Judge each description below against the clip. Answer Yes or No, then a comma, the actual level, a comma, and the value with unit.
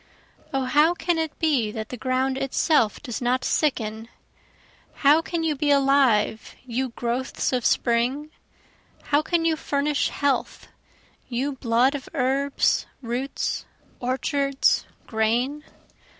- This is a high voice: Yes, very high, 270 Hz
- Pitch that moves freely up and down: No, average, 3.3 semitones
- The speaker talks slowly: Yes, slow, 120 wpm